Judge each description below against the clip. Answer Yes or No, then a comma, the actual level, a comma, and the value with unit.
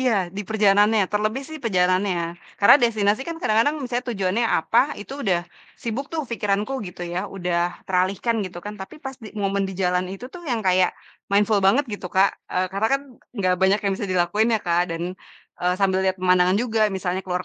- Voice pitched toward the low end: No, high, 200 Hz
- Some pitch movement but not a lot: Yes, average, 3.2 semitones